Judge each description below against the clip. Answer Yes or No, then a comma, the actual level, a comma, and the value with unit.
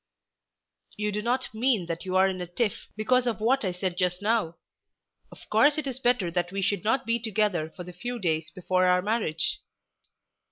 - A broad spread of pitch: No, average, 4.6 semitones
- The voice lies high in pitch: Yes, high, 200 Hz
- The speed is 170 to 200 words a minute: Yes, average, 195 wpm